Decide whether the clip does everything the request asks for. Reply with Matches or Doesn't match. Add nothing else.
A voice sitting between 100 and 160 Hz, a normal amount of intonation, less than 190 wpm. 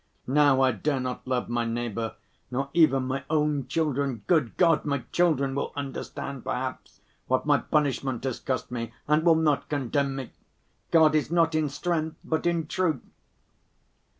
Matches